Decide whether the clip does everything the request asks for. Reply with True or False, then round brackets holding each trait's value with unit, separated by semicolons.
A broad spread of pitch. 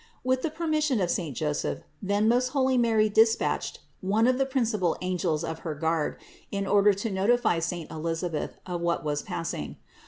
True (6.3 semitones)